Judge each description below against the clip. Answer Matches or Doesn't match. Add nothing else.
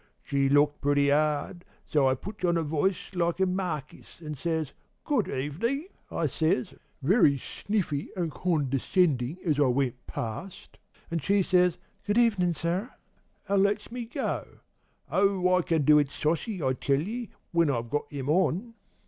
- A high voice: Doesn't match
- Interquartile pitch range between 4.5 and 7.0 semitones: Matches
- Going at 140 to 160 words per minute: Matches